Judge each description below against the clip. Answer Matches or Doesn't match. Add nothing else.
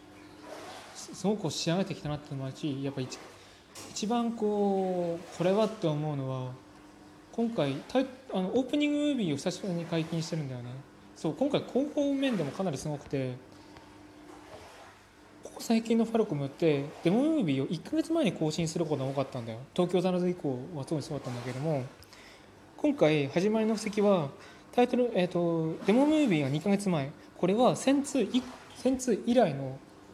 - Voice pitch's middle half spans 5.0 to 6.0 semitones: Doesn't match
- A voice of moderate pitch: Matches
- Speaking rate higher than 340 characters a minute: Matches